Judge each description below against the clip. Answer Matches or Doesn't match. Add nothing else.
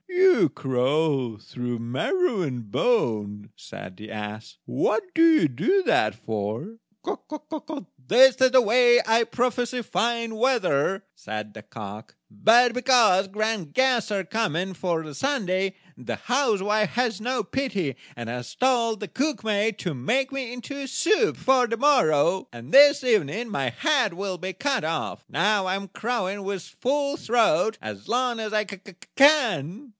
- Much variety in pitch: Matches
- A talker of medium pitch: Doesn't match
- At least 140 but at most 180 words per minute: Matches